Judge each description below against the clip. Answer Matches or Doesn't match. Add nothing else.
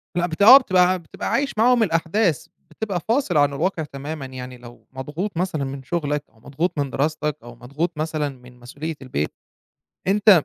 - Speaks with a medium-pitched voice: Matches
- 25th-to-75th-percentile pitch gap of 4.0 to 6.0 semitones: Matches